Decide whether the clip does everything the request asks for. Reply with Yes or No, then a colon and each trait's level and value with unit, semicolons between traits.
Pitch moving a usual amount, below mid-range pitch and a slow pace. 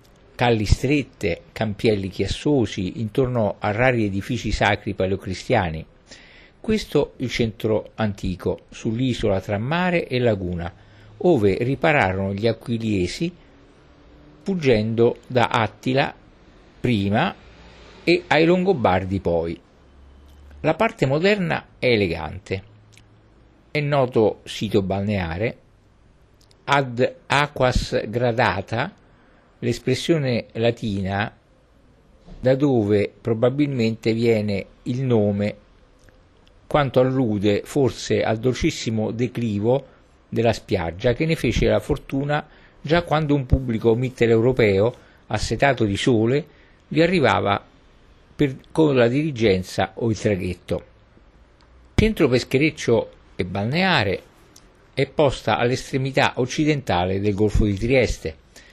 Yes: average, 4.7 semitones; low, 115 Hz; slow, 95 wpm